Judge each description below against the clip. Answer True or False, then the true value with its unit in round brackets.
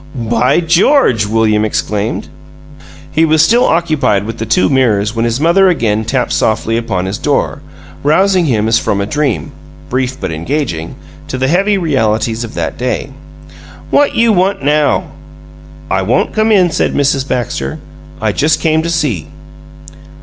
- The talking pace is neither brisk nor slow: True (155 wpm)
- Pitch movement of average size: False (7.0 semitones)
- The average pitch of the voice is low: True (130 Hz)